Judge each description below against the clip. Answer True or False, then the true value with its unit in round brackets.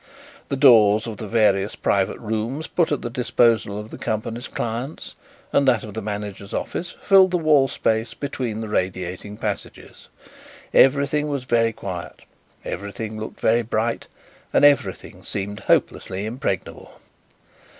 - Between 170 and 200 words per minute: False (140 wpm)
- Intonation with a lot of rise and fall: False (4.1 semitones)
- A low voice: True (110 Hz)